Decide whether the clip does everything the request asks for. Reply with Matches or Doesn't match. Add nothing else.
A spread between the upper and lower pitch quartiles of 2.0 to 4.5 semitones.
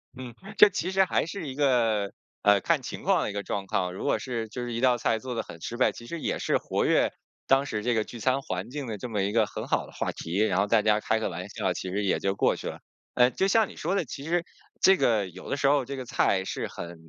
Doesn't match